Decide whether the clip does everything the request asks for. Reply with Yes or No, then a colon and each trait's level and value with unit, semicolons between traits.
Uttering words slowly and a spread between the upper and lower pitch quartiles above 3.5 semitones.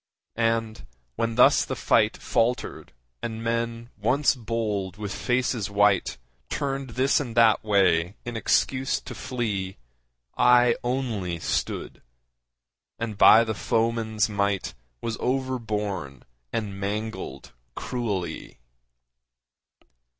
No: slow, 105 wpm; average, 3.0 semitones